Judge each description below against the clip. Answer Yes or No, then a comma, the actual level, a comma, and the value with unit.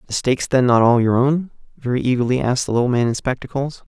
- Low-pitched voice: Yes, low, 125 Hz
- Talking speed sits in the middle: No, fast, 230 wpm